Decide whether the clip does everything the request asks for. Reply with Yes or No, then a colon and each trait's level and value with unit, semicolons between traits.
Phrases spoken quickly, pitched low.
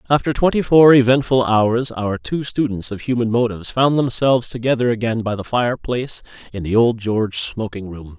No: average, 175 wpm; low, 120 Hz